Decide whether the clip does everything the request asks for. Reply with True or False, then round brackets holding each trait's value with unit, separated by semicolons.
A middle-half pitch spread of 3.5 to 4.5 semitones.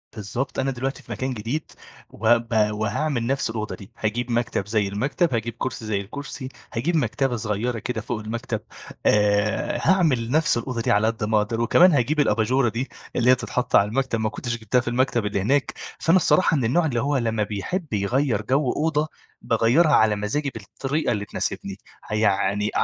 True (3.9 semitones)